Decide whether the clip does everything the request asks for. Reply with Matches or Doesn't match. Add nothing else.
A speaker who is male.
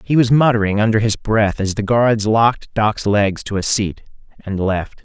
Matches